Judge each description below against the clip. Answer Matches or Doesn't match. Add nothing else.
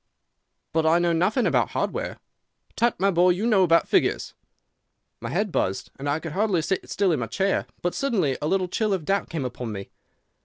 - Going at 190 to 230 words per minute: Matches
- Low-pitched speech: Doesn't match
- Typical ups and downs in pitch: Matches